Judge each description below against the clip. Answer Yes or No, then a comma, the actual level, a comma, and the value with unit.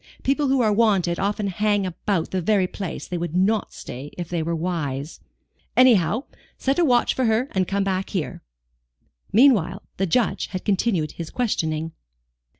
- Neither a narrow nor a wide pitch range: Yes, average, 4.6 semitones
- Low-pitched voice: No, high, 195 Hz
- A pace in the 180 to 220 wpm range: No, average, 170 wpm